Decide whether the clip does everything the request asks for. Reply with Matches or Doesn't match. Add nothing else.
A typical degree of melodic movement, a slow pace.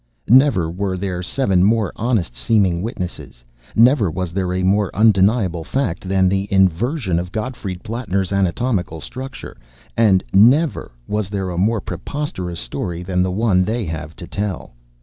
Doesn't match